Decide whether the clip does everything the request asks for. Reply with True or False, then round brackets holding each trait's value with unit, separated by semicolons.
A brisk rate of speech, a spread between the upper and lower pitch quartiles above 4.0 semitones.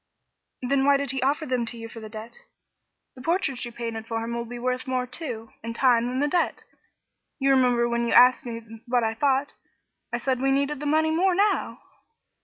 False (210 wpm; 2.9 semitones)